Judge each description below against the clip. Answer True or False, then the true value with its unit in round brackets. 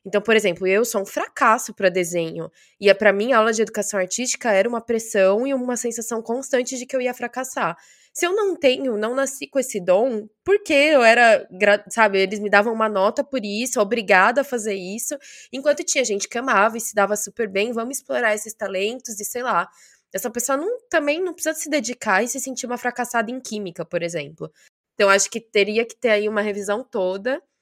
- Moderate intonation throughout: True (4.1 semitones)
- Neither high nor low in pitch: False (230 Hz)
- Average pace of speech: False (215 wpm)